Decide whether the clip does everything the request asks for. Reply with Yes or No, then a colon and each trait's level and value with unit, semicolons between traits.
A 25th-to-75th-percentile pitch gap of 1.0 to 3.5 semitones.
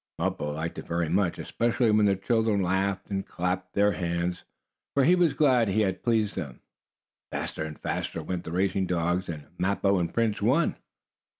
No: average, 3.9 semitones